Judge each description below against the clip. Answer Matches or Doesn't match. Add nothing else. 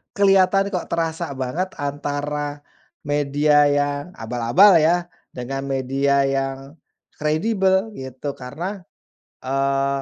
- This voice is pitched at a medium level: Matches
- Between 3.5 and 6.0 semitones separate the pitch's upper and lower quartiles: Matches